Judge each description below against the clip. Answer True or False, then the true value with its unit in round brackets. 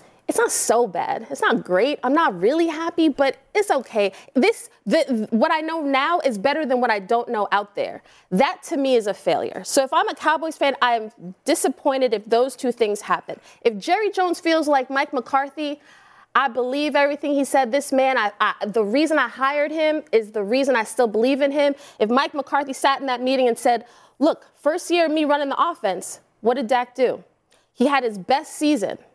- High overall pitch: True (275 Hz)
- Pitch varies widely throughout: False (4.2 semitones)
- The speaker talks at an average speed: False (215 wpm)